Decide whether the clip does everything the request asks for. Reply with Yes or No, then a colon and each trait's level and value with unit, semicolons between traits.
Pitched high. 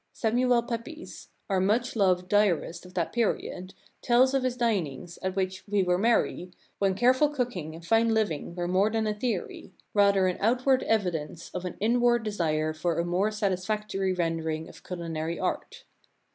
Yes: high, 195 Hz